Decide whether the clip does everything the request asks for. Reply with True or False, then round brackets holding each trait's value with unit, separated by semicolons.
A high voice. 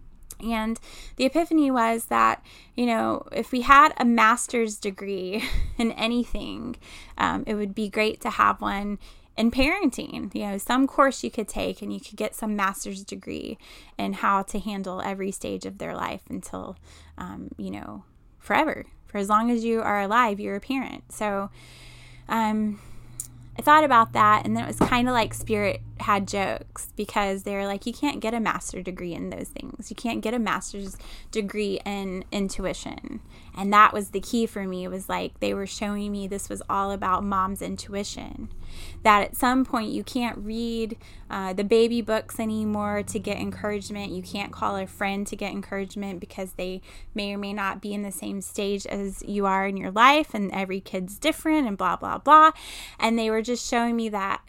True (205 Hz)